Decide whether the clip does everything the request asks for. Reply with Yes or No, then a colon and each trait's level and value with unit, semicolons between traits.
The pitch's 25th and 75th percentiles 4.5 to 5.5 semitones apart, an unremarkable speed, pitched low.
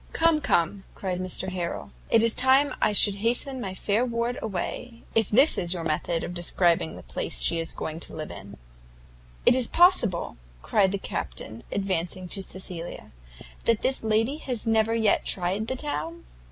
No: average, 5.0 semitones; average, 175 wpm; high, 200 Hz